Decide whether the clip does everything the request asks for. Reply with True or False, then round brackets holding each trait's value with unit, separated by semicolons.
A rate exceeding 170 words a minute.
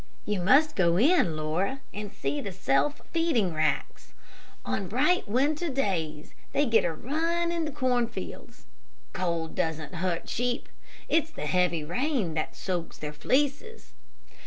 False (140 wpm)